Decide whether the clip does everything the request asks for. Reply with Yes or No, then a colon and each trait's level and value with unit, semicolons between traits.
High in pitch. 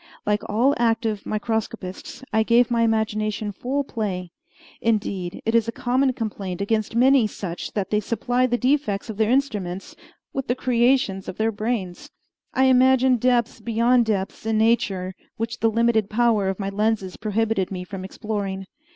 Yes: high, 220 Hz